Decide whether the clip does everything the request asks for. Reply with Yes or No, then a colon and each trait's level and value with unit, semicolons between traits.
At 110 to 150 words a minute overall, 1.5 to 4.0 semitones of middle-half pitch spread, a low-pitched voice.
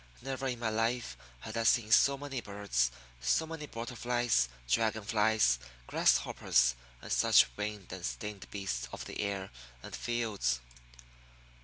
Yes: average, 145 wpm; average, 3.6 semitones; low, 110 Hz